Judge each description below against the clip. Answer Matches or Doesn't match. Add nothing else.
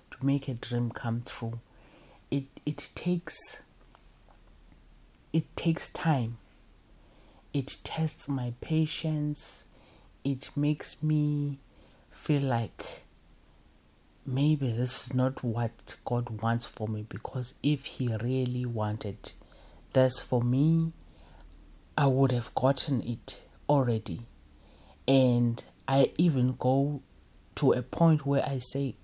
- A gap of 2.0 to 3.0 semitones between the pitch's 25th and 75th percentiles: Doesn't match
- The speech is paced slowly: Matches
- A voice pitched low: Matches